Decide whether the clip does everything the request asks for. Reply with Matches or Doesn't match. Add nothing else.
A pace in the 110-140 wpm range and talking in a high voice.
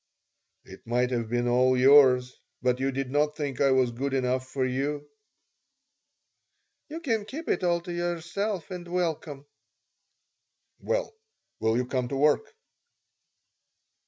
Doesn't match